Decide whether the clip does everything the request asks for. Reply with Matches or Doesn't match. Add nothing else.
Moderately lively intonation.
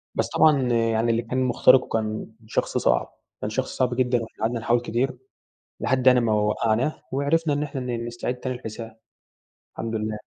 Doesn't match